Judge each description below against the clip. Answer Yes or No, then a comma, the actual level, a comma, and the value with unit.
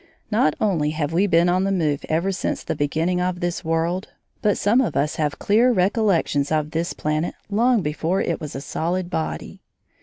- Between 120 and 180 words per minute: No, average, 190 wpm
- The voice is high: No, medium, 175 Hz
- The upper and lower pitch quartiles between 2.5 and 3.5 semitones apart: No, average, 3.9 semitones